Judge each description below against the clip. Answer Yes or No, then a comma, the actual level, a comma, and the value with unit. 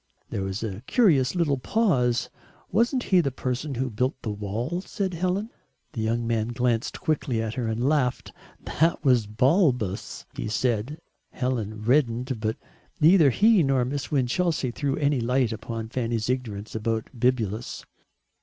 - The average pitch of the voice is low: Yes, low, 125 Hz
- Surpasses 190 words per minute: No, average, 150 wpm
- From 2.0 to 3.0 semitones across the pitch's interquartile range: No, average, 4.7 semitones